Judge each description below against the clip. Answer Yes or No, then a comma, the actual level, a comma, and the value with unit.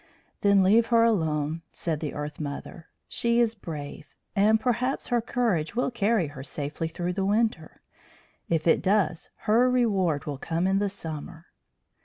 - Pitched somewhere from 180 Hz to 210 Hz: Yes, high, 190 Hz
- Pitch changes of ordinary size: No, wide, 6.1 semitones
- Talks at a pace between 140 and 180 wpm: Yes, average, 160 wpm